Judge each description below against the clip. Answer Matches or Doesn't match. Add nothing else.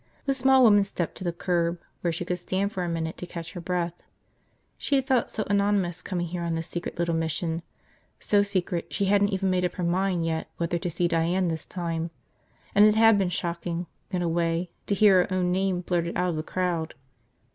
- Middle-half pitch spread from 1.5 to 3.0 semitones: Matches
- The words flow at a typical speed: Doesn't match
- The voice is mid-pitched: Matches